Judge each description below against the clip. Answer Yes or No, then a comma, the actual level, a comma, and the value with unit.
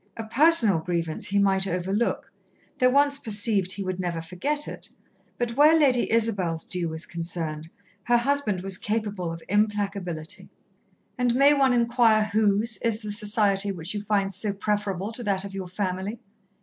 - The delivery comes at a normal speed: Yes, average, 160 wpm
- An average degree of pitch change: Yes, average, 3.9 semitones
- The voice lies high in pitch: Yes, high, 205 Hz